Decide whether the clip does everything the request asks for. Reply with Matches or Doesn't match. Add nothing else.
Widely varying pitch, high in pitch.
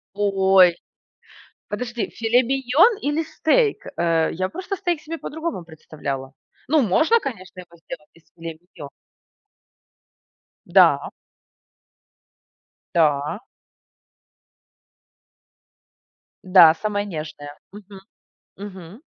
Matches